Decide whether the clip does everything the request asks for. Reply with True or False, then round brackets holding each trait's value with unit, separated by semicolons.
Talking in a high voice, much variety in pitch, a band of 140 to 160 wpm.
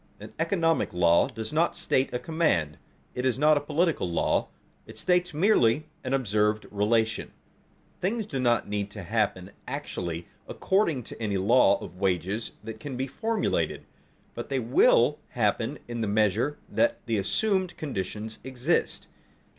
False (120 Hz; 7.3 semitones; 150 wpm)